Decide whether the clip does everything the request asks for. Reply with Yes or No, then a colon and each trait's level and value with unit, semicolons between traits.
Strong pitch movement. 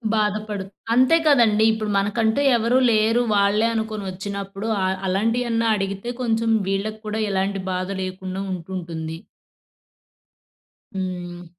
No: average, 2.8 semitones